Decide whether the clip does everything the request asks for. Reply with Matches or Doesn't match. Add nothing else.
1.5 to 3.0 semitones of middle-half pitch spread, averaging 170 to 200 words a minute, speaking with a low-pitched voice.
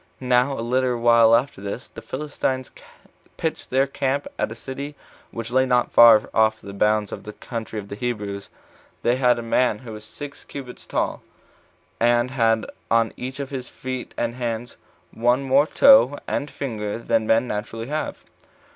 Matches